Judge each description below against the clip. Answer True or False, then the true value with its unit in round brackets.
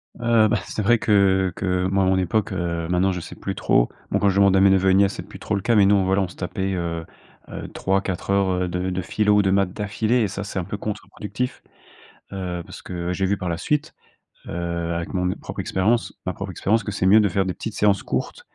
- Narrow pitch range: True (2.2 semitones)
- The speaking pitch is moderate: False (95 Hz)